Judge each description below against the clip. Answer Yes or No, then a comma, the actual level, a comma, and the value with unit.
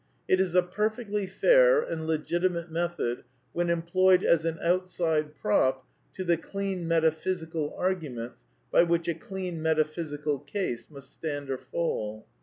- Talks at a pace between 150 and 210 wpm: No, average, 140 wpm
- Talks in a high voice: No, medium, 170 Hz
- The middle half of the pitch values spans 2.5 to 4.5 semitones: Yes, average, 3.2 semitones